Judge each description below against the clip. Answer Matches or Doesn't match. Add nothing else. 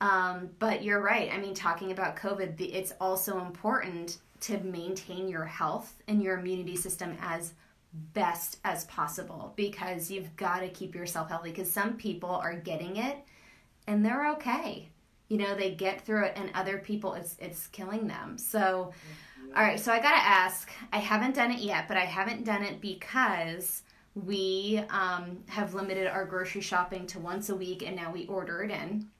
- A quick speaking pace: Doesn't match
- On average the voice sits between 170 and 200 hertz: Matches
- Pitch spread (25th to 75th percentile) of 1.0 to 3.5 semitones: Matches